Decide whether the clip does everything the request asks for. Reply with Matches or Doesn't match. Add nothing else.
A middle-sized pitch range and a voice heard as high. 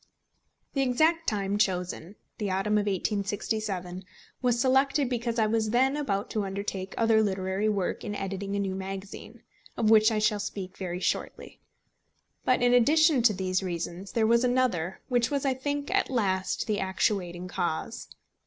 Matches